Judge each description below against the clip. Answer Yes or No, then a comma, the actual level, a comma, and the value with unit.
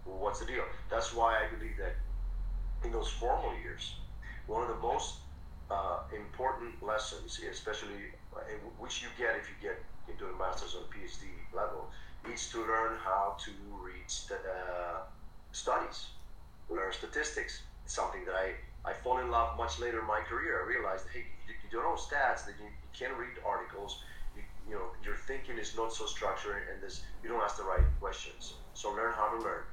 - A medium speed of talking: No, fast, 190 wpm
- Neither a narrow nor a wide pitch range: No, wide, 7.2 semitones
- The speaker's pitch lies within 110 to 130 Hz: No, low, 100 Hz